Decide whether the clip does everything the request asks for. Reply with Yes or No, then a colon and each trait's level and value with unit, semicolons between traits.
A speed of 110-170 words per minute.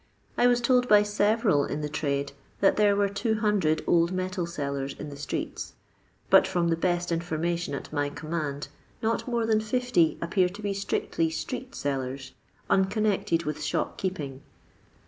Yes: average, 160 wpm